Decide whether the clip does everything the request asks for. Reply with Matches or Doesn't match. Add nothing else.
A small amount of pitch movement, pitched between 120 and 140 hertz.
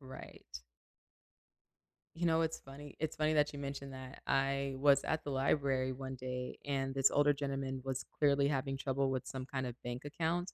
Matches